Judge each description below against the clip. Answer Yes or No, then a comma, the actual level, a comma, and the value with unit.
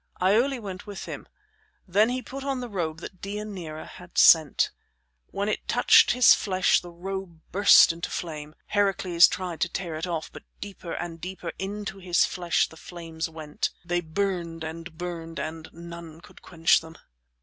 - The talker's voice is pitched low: No, medium, 175 Hz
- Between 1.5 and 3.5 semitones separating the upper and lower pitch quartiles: Yes, average, 3.1 semitones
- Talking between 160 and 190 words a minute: Yes, average, 170 wpm